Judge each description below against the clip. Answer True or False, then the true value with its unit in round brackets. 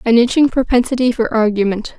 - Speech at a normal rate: True (150 wpm)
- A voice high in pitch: True (235 Hz)